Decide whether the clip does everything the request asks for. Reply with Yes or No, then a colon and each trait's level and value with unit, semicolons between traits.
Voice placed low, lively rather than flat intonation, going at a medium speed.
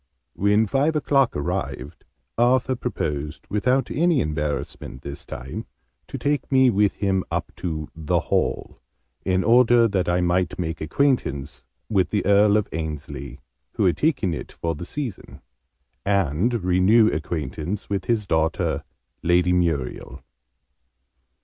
No: very low, 95 Hz; wide, 6.8 semitones; slow, 130 wpm